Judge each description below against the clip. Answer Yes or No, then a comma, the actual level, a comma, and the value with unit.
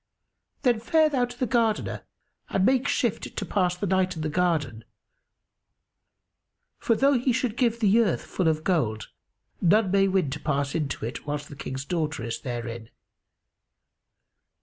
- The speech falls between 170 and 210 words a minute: No, average, 160 wpm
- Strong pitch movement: Yes, wide, 8.0 semitones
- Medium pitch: Yes, medium, 180 Hz